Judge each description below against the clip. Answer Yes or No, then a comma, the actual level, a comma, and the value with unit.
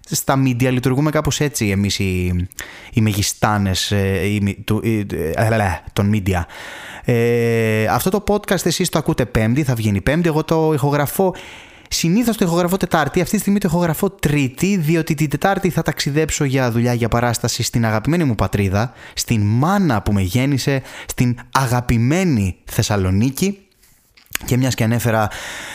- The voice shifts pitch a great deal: Yes, wide, 7.0 semitones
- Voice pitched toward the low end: Yes, low, 125 Hz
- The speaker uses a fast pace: No, average, 140 wpm